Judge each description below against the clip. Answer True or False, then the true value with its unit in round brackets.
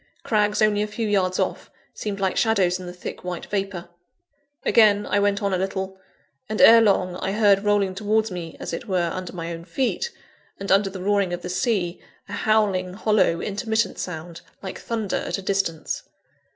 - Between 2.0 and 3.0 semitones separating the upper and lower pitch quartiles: True (2.5 semitones)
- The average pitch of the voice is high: True (195 Hz)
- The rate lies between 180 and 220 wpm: True (190 wpm)